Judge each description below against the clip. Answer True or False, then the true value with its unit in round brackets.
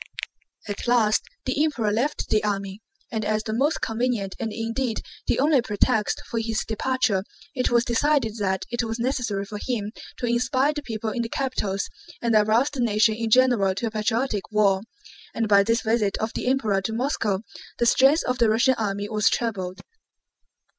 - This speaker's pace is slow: False (180 wpm)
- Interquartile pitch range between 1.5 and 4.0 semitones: True (3.1 semitones)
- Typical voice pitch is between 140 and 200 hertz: False (225 Hz)